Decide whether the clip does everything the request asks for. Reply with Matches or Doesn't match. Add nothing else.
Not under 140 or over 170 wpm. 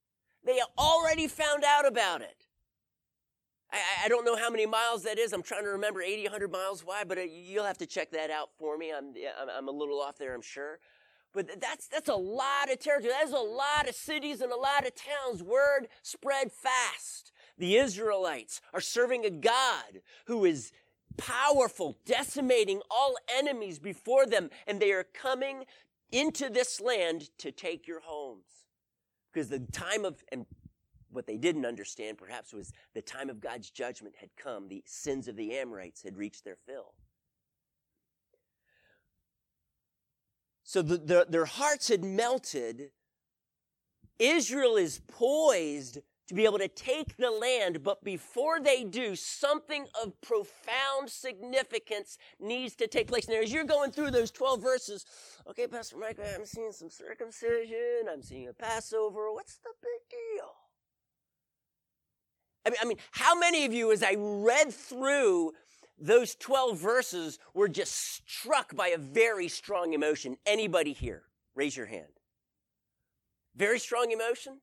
Matches